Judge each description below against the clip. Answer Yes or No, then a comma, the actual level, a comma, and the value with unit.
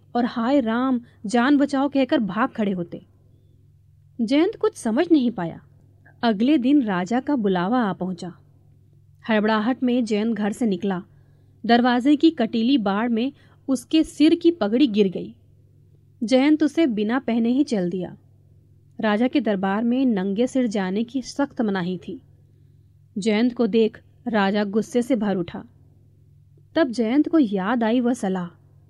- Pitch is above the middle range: Yes, high, 220 Hz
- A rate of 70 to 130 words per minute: No, average, 145 wpm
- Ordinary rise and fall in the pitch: No, wide, 7.4 semitones